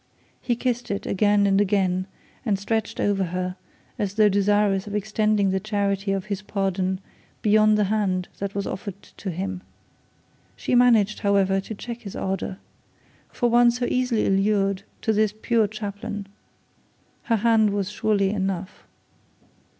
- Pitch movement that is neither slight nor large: No, narrow, 1.8 semitones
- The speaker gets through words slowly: No, average, 150 wpm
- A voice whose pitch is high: Yes, high, 205 Hz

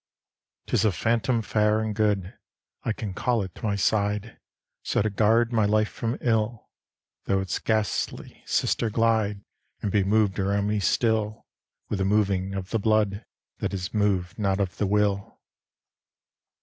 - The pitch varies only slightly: Yes, narrow, 1.9 semitones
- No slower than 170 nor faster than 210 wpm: No, average, 160 wpm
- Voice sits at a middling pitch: No, low, 105 Hz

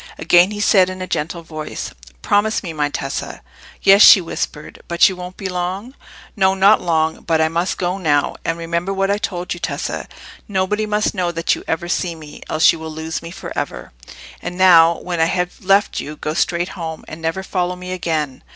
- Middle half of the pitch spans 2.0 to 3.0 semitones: Yes, average, 2.7 semitones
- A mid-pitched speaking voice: Yes, medium, 175 Hz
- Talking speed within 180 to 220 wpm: Yes, fast, 205 wpm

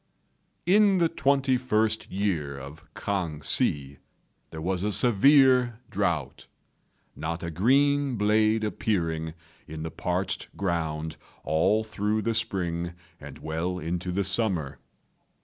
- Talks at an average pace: No, slow, 120 wpm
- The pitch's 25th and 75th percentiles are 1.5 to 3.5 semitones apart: No, wide, 5.6 semitones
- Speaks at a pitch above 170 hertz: No, very low, 95 Hz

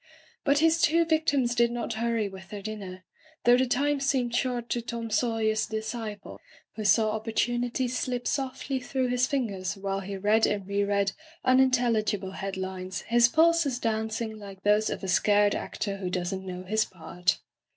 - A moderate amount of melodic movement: Yes, average, 3.8 semitones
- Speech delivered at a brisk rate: No, average, 170 wpm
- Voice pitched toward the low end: No, high, 220 Hz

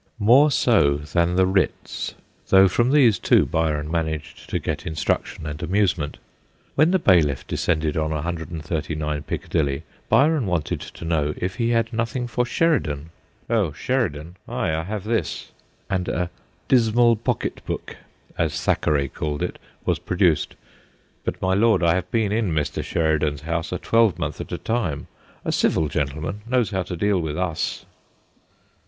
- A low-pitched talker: Yes, very low, 90 Hz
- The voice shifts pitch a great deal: Yes, wide, 6.3 semitones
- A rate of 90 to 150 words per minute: No, average, 160 wpm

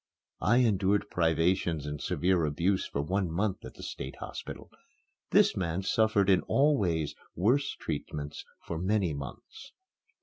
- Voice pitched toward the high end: No, very low, 90 Hz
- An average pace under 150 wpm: Yes, average, 140 wpm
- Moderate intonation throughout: Yes, average, 4.0 semitones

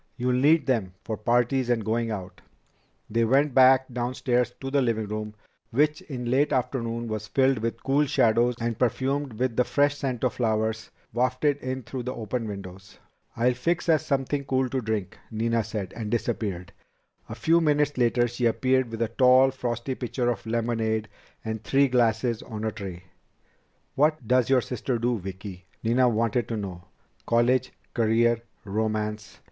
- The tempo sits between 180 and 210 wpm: No, average, 165 wpm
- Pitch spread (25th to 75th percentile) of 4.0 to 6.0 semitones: No, average, 2.8 semitones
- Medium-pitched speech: No, low, 120 Hz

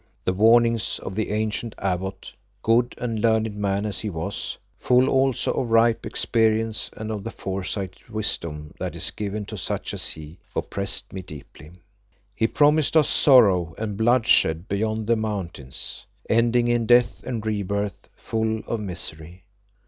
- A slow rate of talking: No, average, 150 wpm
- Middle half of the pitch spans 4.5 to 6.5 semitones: No, average, 3.1 semitones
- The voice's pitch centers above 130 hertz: No, low, 110 Hz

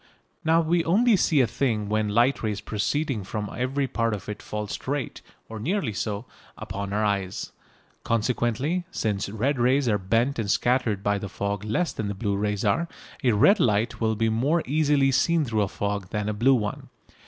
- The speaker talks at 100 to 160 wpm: No, average, 190 wpm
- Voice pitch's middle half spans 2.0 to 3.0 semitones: No, average, 4.9 semitones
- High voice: No, low, 115 Hz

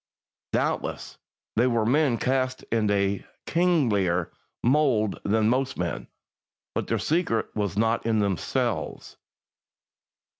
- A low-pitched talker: Yes, low, 115 Hz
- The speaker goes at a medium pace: No, slow, 110 wpm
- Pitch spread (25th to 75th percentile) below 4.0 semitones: No, average, 4.3 semitones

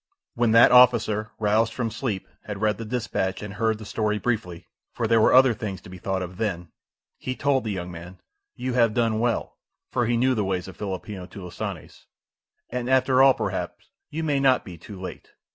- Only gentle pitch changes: No, average, 4.3 semitones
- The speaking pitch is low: Yes, low, 110 Hz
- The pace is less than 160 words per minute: No, average, 200 wpm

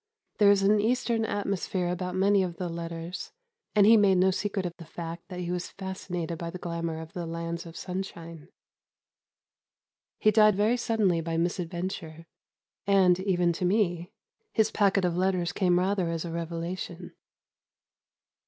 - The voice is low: No, medium, 180 Hz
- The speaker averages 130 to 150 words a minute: No, average, 160 wpm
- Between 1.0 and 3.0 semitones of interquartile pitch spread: Yes, narrow, 2.6 semitones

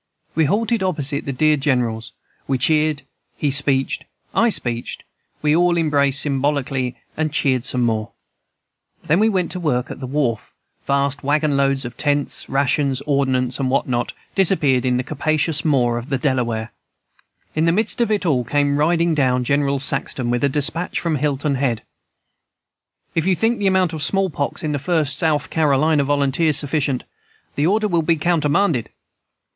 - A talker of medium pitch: Yes, medium, 145 Hz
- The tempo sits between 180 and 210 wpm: No, average, 170 wpm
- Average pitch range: Yes, average, 3.4 semitones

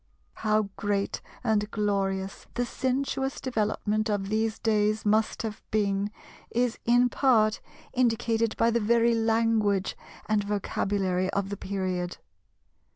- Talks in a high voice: Yes, high, 215 Hz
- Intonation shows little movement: Yes, narrow, 2.3 semitones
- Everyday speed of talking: No, slow, 120 wpm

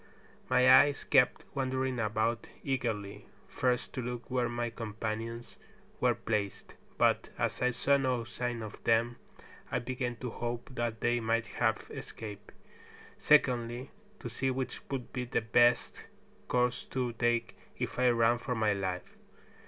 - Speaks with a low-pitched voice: Yes, low, 120 Hz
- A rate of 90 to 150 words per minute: Yes, average, 145 wpm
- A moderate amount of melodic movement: No, narrow, 1.8 semitones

